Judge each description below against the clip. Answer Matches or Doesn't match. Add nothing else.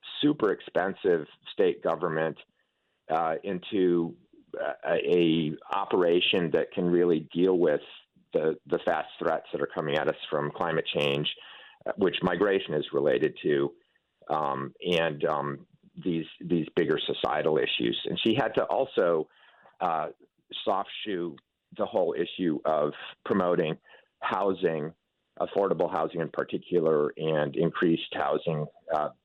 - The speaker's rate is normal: Doesn't match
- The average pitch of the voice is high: Matches